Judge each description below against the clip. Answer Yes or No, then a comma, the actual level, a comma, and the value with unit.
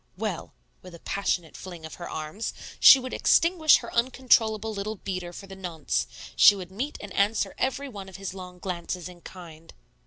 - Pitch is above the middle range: Yes, high, 195 Hz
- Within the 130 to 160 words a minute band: No, average, 185 wpm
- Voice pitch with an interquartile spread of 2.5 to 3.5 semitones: No, average, 3.9 semitones